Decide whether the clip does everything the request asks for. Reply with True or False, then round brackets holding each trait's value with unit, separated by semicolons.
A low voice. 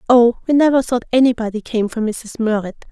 False (235 Hz)